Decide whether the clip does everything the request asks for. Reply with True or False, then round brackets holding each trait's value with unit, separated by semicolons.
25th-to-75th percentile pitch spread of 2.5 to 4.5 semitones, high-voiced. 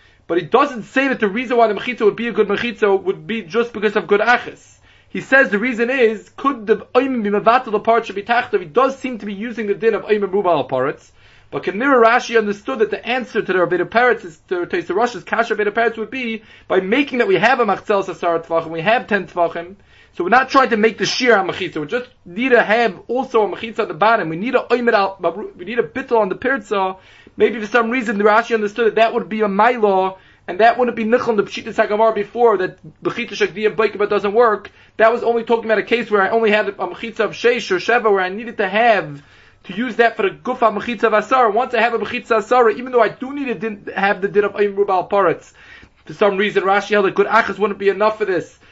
True (2.9 semitones; 220 Hz)